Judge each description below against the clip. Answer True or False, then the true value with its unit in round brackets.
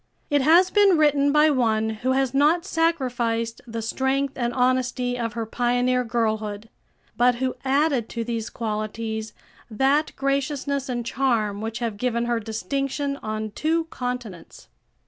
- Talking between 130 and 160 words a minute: True (145 wpm)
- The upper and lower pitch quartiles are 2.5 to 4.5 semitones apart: True (3.5 semitones)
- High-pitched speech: True (250 Hz)